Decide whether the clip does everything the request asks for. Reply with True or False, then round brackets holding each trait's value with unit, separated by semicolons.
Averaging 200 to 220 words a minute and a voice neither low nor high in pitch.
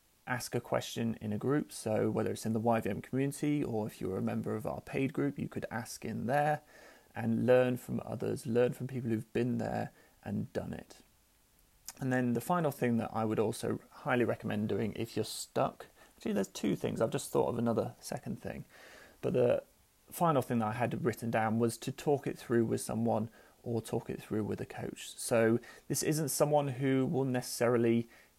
False (205 wpm; 115 Hz)